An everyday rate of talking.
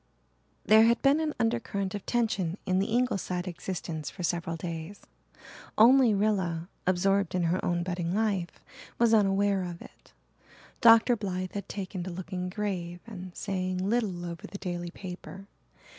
Yes: average, 150 wpm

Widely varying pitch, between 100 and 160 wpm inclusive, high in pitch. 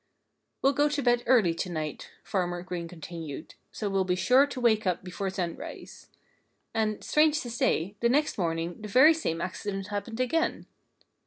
No: wide, 6.1 semitones; average, 170 wpm; high, 200 Hz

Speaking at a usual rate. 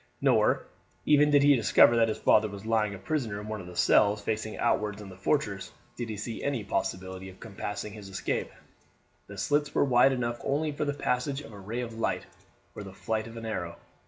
No: fast, 215 wpm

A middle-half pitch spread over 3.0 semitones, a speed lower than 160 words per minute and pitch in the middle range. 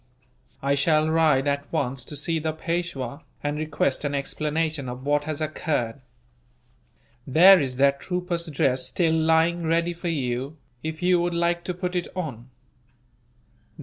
Yes: average, 3.4 semitones; average, 150 wpm; medium, 155 Hz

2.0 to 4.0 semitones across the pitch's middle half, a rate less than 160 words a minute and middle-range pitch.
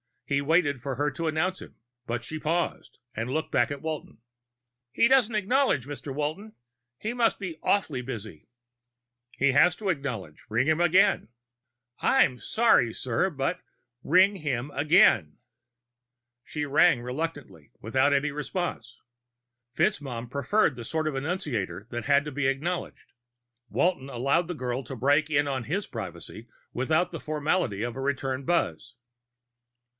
No: average, 5.0 semitones; average, 150 wpm; medium, 145 Hz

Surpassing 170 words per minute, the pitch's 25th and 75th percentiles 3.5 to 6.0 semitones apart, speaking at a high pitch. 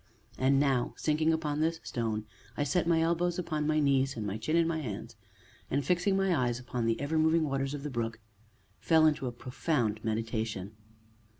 No: average, 190 wpm; average, 5.2 semitones; medium, 140 Hz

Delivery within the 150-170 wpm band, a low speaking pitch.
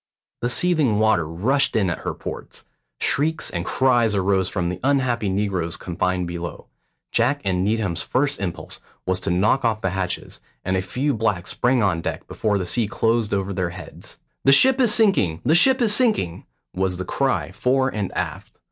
No: average, 185 wpm; low, 105 Hz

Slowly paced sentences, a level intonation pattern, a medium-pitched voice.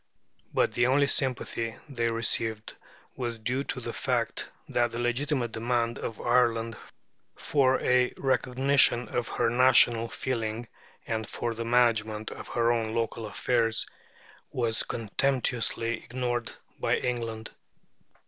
No: slow, 125 wpm; narrow, 1.7 semitones; low, 120 Hz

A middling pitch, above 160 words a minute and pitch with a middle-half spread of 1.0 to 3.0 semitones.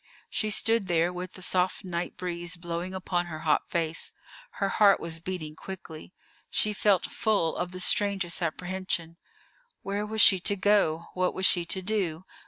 Yes: medium, 180 Hz; average, 170 wpm; narrow, 2.5 semitones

